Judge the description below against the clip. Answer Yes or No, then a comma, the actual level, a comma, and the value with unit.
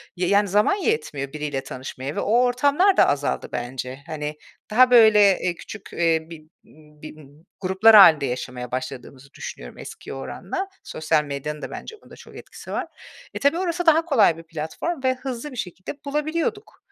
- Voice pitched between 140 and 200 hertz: Yes, medium, 185 Hz